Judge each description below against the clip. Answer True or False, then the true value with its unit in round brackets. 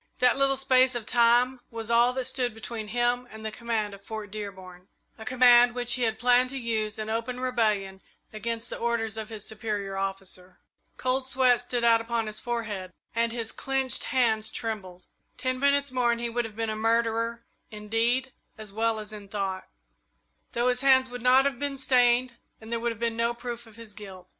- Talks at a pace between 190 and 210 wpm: True (200 wpm)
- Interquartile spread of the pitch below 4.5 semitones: True (2.5 semitones)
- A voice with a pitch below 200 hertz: False (230 Hz)